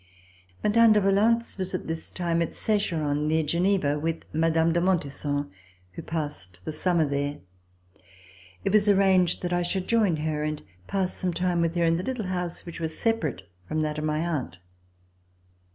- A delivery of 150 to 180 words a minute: Yes, average, 175 wpm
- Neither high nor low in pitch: Yes, medium, 170 Hz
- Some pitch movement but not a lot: Yes, average, 3.6 semitones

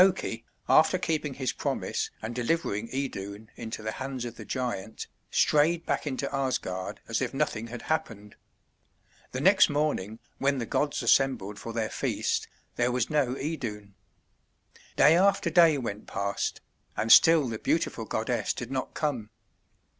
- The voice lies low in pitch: Yes, low, 125 Hz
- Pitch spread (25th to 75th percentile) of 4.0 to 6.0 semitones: Yes, average, 5.1 semitones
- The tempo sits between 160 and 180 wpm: No, average, 150 wpm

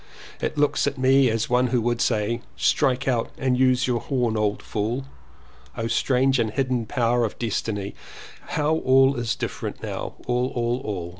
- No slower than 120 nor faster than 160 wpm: No, average, 170 wpm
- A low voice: Yes, low, 125 Hz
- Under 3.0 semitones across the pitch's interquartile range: Yes, narrow, 2.4 semitones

